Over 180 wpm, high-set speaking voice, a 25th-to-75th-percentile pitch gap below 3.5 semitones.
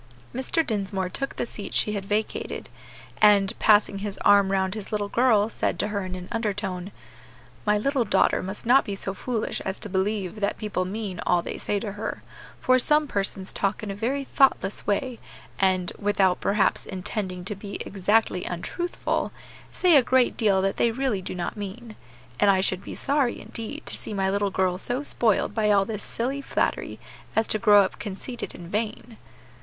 Yes: average, 190 wpm; high, 205 Hz; average, 2.8 semitones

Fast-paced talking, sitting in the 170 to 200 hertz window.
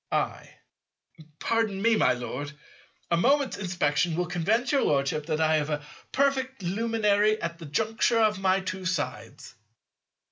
No: average, 145 wpm; high, 190 Hz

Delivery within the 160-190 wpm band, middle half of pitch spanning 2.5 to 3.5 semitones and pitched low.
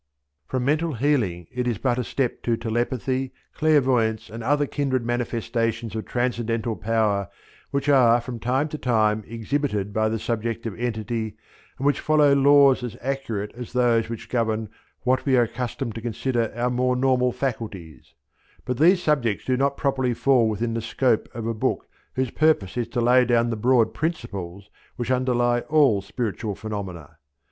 Yes: average, 165 wpm; average, 2.8 semitones; low, 120 Hz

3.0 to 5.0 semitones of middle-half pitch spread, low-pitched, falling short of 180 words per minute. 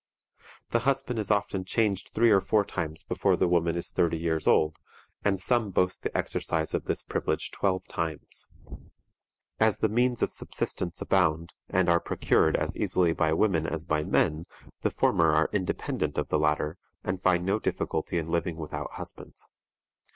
Yes: average, 3.8 semitones; very low, 90 Hz; average, 170 wpm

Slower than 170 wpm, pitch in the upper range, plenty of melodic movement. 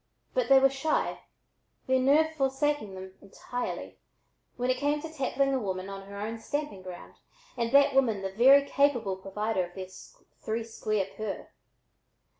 Yes: average, 160 wpm; high, 245 Hz; wide, 5.8 semitones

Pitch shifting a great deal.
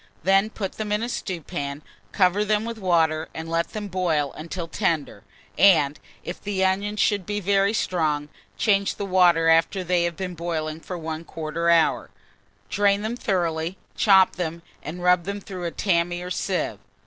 No: average, 3.3 semitones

